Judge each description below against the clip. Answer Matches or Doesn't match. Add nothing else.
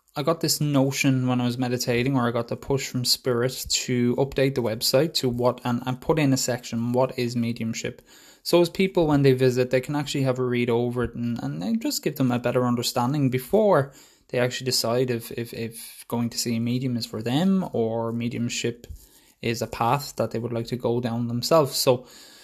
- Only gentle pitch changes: Matches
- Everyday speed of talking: Doesn't match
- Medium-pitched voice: Doesn't match